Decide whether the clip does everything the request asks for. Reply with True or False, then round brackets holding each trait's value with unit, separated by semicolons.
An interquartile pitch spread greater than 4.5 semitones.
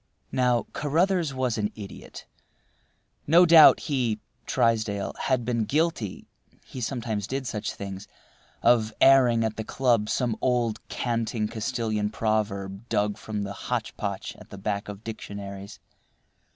False (3.3 semitones)